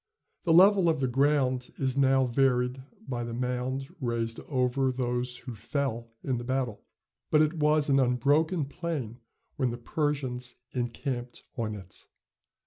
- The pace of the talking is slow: No, average, 145 wpm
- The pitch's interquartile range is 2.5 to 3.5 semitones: Yes, average, 2.8 semitones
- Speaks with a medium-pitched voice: No, low, 130 Hz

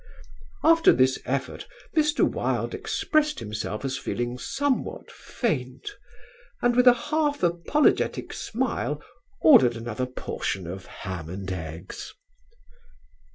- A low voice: Yes, low, 130 Hz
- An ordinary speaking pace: No, slow, 110 wpm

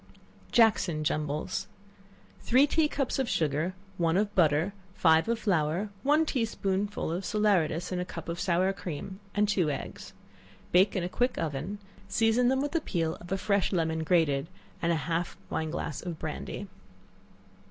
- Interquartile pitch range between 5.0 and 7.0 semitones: No, average, 4.6 semitones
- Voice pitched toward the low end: No, medium, 180 Hz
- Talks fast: No, average, 165 wpm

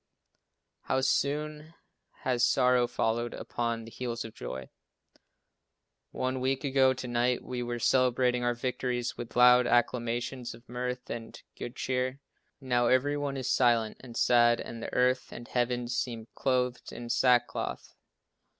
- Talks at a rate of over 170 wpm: No, average, 145 wpm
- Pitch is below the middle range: Yes, low, 125 Hz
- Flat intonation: Yes, narrow, 1.3 semitones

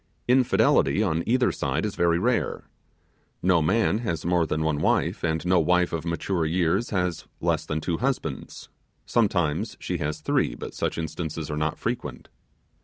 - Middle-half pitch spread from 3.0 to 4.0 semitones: Yes, average, 3.4 semitones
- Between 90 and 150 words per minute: No, average, 165 wpm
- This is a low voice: Yes, very low, 85 Hz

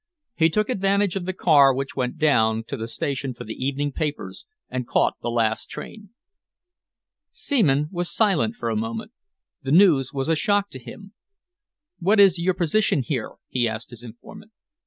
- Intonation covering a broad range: Yes, wide, 7.4 semitones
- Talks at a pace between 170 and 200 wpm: Yes, average, 175 wpm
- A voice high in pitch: No, medium, 150 Hz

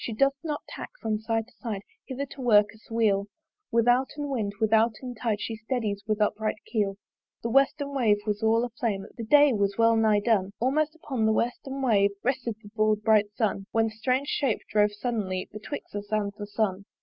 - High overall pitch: Yes, high, 220 Hz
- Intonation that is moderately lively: Yes, average, 3.0 semitones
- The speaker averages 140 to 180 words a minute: No, average, 195 wpm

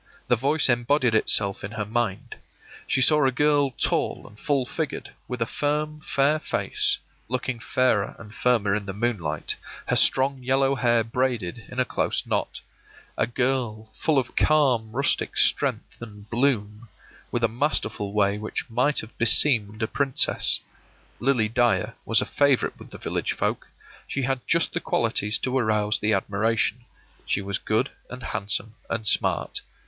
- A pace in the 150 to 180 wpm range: Yes, average, 165 wpm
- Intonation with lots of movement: No, average, 3.8 semitones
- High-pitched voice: No, low, 120 Hz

